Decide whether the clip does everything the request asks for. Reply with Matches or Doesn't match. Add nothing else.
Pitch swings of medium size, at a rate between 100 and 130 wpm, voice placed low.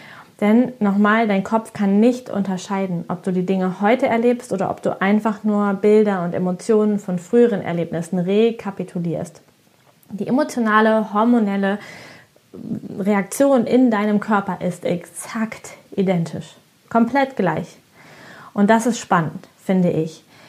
Doesn't match